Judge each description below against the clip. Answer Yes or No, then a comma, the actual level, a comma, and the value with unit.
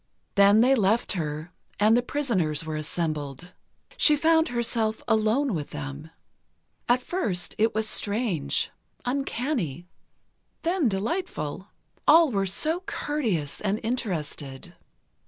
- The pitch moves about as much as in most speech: No, wide, 7.9 semitones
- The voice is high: Yes, high, 215 Hz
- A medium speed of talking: No, slow, 115 wpm